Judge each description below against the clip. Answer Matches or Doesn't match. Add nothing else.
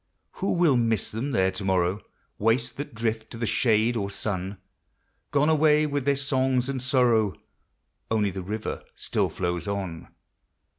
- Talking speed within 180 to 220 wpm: Doesn't match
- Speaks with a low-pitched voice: Matches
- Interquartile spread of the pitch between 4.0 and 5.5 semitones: Matches